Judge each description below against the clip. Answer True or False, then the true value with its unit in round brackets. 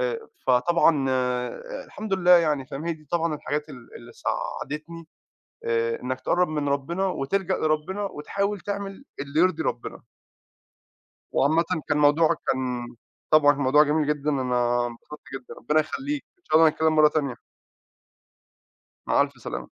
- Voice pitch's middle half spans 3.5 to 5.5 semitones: True (3.9 semitones)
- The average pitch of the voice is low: False (150 Hz)